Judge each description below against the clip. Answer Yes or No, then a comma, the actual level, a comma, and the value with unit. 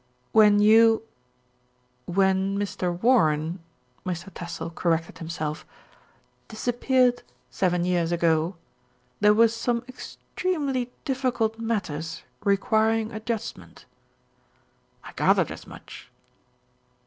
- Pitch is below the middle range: No, high, 210 Hz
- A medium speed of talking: No, slow, 95 wpm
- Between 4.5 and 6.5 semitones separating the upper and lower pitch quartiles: Yes, average, 5.0 semitones